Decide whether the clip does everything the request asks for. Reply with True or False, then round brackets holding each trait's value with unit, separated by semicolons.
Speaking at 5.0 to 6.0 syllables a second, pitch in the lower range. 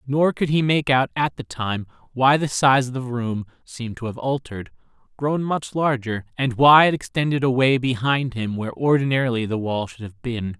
True (5.1 syllables/s; 125 Hz)